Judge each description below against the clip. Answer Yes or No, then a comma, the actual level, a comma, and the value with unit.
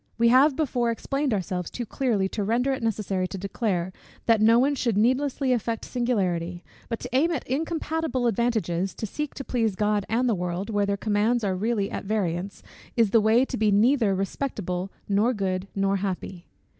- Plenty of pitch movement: No, average, 4.1 semitones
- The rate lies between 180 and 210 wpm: Yes, average, 185 wpm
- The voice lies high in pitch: Yes, high, 220 Hz